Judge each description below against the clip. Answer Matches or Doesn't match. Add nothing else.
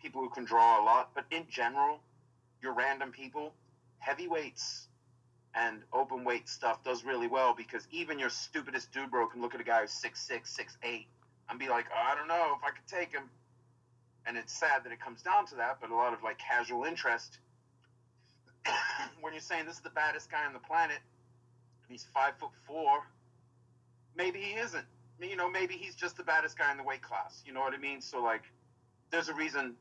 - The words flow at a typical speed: Doesn't match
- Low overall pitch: Matches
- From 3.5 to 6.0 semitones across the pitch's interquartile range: Matches